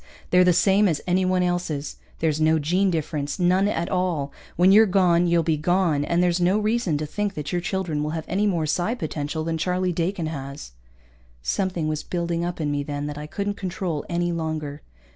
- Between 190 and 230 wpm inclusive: Yes, average, 200 wpm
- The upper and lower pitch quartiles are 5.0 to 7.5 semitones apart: No, average, 3.1 semitones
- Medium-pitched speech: Yes, medium, 170 Hz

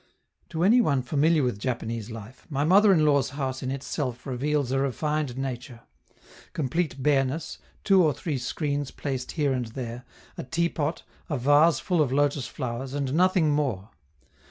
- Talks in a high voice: No, medium, 140 Hz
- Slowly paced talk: No, average, 160 wpm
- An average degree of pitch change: Yes, average, 3.2 semitones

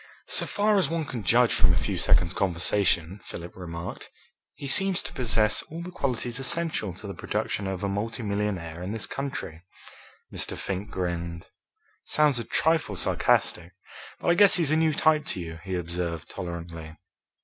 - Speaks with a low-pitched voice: Yes, low, 100 Hz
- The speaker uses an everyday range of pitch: No, wide, 8.5 semitones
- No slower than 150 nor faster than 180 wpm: Yes, average, 170 wpm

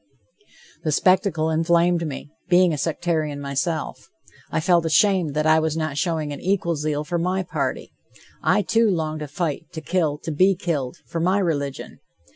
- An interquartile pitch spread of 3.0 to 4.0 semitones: No, narrow, 2.6 semitones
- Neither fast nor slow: Yes, average, 170 wpm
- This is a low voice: No, medium, 160 Hz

